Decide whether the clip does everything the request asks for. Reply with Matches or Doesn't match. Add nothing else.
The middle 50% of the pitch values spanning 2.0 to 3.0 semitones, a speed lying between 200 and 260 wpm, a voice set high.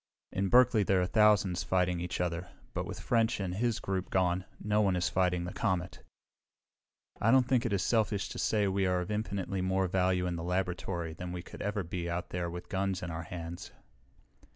Doesn't match